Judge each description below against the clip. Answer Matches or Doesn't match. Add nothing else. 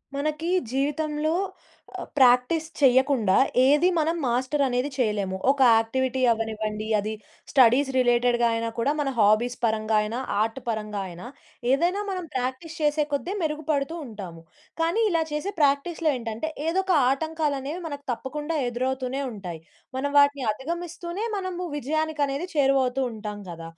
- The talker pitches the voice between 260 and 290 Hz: Matches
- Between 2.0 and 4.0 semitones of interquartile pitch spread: Doesn't match